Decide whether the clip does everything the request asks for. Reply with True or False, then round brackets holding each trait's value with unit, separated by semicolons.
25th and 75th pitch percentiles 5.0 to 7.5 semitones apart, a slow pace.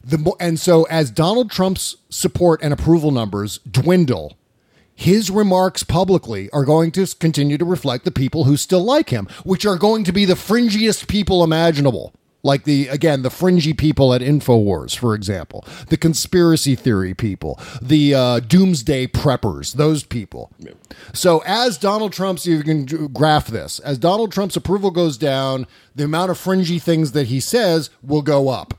False (5.4 semitones; 165 wpm)